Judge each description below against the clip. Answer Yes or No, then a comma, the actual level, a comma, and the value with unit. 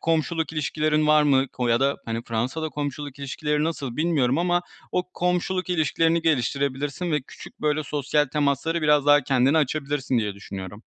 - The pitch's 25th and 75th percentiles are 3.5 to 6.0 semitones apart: No, average, 3.0 semitones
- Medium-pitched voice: Yes, medium, 145 Hz